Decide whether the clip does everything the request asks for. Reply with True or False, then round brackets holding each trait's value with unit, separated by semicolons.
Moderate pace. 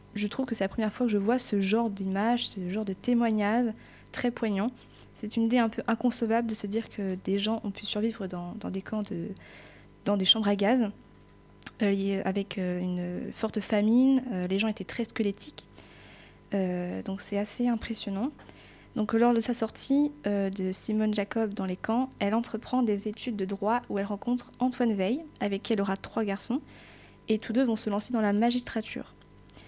True (195 wpm)